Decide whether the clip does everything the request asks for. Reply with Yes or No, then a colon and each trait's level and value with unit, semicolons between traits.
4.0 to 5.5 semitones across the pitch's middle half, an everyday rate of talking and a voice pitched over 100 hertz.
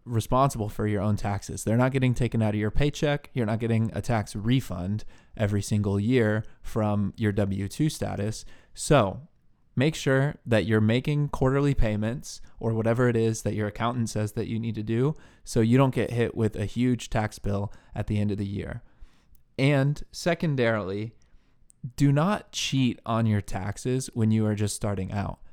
No: average, 3.2 semitones; average, 185 wpm; low, 110 Hz